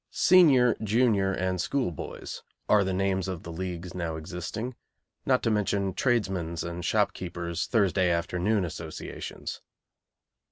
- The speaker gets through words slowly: Yes, slow, 125 wpm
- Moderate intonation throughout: Yes, average, 3.7 semitones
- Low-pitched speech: Yes, very low, 95 Hz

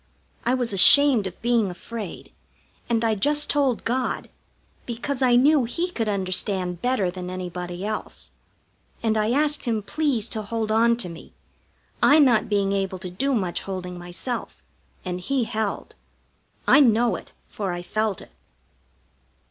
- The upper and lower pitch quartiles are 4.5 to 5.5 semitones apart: Yes, average, 4.9 semitones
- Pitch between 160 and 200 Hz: No, high, 220 Hz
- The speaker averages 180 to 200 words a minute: No, average, 155 wpm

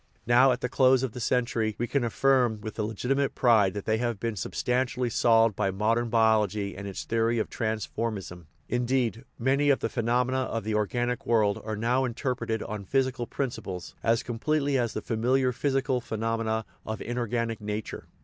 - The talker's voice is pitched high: No, low, 115 Hz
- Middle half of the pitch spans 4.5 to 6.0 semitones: No, narrow, 2.4 semitones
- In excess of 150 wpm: Yes, average, 180 wpm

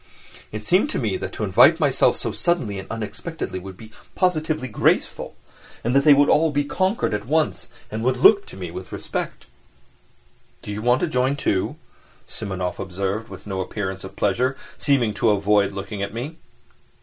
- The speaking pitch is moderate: No, low, 110 Hz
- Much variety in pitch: Yes, wide, 6.6 semitones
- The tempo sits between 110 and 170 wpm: No, average, 180 wpm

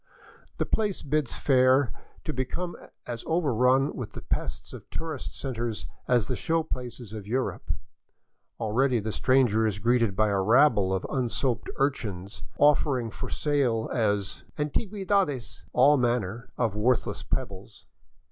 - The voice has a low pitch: Yes, low, 125 Hz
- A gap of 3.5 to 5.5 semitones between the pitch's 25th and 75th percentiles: Yes, average, 4.2 semitones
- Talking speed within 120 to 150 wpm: Yes, average, 140 wpm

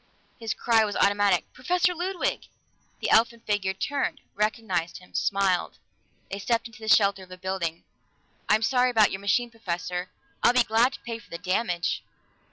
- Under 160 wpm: No, average, 170 wpm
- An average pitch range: Yes, average, 3.7 semitones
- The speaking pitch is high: Yes, high, 210 Hz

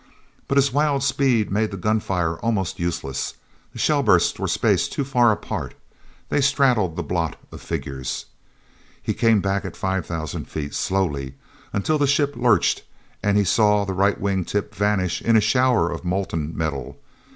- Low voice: Yes, low, 100 Hz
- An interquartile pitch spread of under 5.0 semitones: No, wide, 5.6 semitones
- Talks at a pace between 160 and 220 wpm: Yes, average, 165 wpm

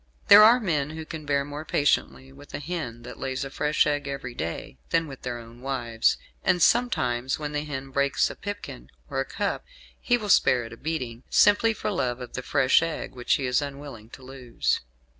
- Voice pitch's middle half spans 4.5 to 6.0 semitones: No, average, 4.0 semitones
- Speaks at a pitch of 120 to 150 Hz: Yes, medium, 140 Hz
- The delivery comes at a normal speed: No, fast, 210 wpm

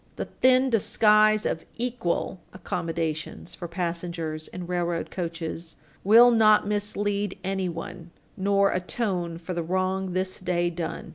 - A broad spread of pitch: No, average, 3.3 semitones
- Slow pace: Yes, slow, 125 wpm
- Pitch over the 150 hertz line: Yes, medium, 185 Hz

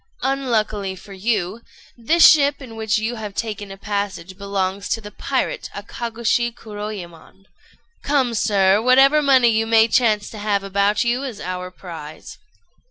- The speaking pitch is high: Yes, high, 215 Hz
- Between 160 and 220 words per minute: No, average, 150 wpm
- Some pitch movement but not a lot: Yes, average, 3.3 semitones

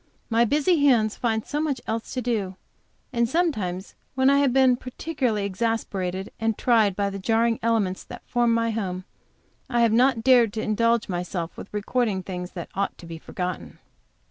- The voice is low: No, high, 225 Hz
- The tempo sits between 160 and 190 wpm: Yes, average, 175 wpm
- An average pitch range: Yes, average, 4.0 semitones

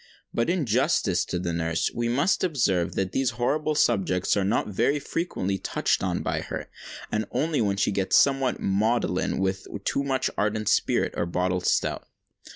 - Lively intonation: Yes, wide, 6.1 semitones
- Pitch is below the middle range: Yes, low, 110 Hz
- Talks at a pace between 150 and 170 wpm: Yes, average, 165 wpm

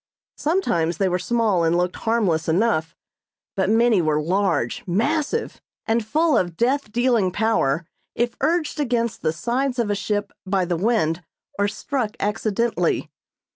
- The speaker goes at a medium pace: Yes, average, 145 wpm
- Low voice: No, high, 210 Hz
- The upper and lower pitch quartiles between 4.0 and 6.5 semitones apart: Yes, average, 5.1 semitones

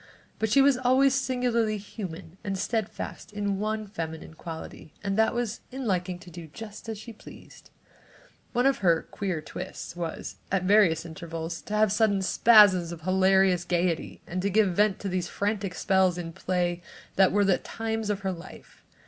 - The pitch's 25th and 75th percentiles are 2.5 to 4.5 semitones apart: Yes, average, 3.5 semitones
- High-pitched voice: Yes, high, 195 Hz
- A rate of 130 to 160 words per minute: No, average, 175 wpm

